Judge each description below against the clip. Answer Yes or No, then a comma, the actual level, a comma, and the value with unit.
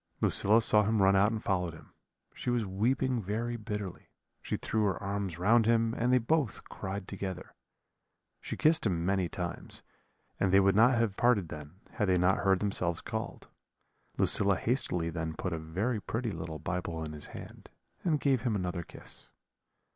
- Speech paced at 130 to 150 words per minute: No, average, 175 wpm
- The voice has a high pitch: No, low, 100 Hz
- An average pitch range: Yes, average, 4.2 semitones